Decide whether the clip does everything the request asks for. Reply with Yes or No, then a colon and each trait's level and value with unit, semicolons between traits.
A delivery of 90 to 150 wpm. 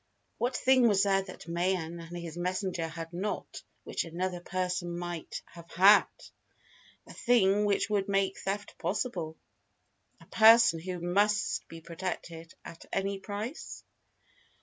Yes: slow, 135 wpm